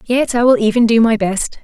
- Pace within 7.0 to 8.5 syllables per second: No, 5.3 syllables/s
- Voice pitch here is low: No, high, 230 Hz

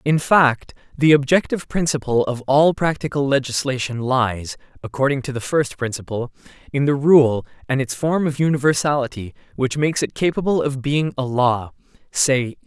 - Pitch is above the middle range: No, low, 135 Hz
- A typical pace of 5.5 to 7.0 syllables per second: No, 4.6 syllables/s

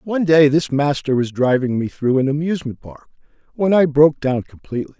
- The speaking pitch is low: No, medium, 145 Hz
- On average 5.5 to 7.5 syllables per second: Yes, 5.9 syllables/s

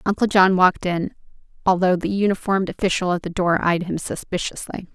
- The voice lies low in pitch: No, medium, 185 Hz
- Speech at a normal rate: Yes, average, 170 wpm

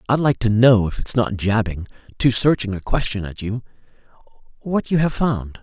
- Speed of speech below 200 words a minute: Yes, average, 180 wpm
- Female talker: No, male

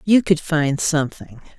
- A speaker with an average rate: Yes, average, 150 wpm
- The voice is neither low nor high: Yes, medium, 160 Hz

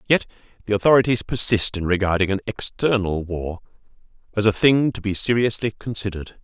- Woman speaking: No, male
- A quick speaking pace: No, average, 150 wpm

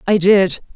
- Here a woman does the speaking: Yes, female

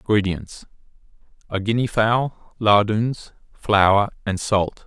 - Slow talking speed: Yes, slow, 85 wpm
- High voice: No, low, 105 Hz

